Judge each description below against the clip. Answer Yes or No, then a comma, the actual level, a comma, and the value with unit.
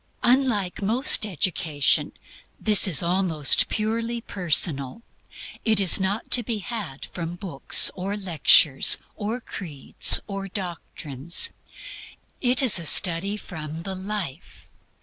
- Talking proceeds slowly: Yes, slow, 115 wpm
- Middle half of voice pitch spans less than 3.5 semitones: No, average, 4.4 semitones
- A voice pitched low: No, high, 190 Hz